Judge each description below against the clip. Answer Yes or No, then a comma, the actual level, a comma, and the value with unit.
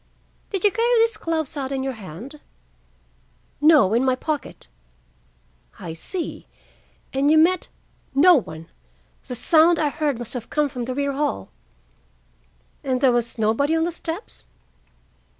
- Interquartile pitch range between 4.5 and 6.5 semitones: Yes, average, 4.8 semitones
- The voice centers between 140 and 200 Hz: No, very high, 280 Hz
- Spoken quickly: No, average, 150 wpm